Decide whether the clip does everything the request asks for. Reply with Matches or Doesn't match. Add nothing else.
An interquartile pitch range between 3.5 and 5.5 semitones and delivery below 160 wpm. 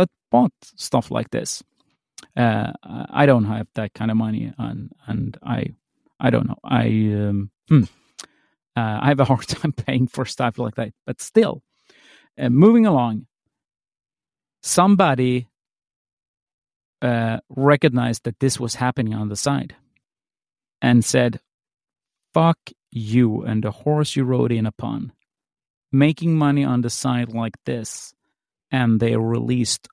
Matches